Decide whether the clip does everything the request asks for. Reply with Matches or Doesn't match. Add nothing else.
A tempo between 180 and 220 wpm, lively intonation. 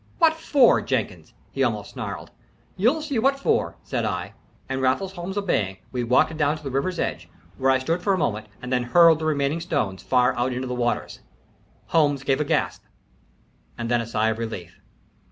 Matches